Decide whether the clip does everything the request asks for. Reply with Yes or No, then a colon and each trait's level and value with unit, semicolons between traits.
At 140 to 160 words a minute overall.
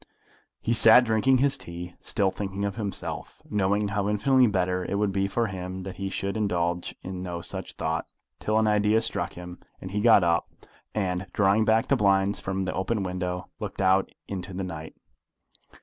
No: average, 185 wpm